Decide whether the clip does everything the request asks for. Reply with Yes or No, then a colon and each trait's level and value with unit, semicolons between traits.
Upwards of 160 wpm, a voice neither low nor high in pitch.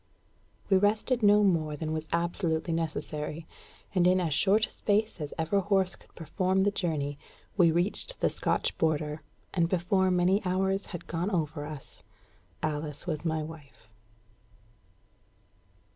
No: average, 145 wpm; medium, 170 Hz